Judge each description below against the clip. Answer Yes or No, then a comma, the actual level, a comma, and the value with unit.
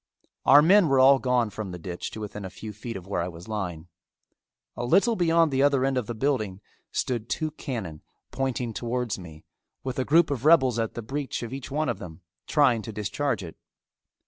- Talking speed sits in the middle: No, fast, 210 wpm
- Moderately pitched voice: No, low, 120 Hz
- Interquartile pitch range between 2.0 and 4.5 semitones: No, average, 5.0 semitones